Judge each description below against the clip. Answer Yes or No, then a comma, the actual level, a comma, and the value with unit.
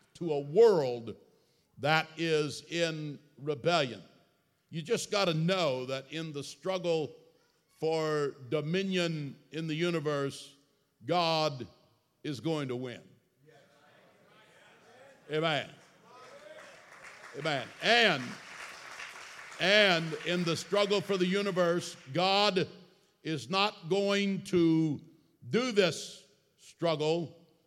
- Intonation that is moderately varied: Yes, average, 3.9 semitones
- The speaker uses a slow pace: Yes, slow, 95 wpm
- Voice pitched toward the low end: No, medium, 165 Hz